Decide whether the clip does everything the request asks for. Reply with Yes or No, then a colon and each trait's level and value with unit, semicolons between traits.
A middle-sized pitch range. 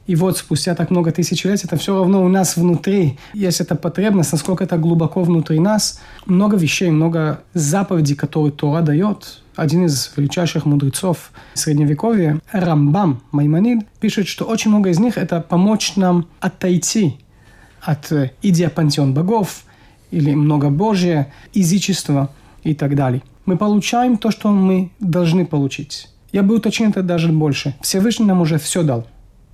Yes: average, 4.4 semitones